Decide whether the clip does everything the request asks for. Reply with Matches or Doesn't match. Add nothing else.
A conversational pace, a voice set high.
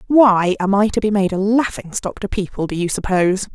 Doesn't match